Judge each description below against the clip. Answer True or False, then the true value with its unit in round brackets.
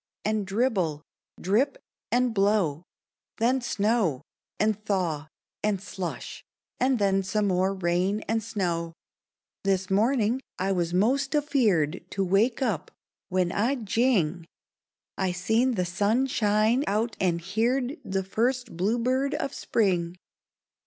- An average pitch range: True (4.4 semitones)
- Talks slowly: True (125 wpm)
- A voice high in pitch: True (205 Hz)